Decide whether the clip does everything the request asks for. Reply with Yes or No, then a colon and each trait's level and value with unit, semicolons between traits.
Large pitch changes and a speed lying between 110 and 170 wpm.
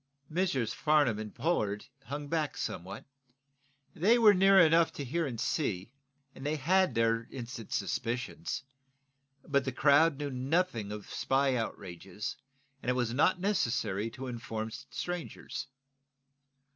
Yes: wide, 6.2 semitones; slow, 135 wpm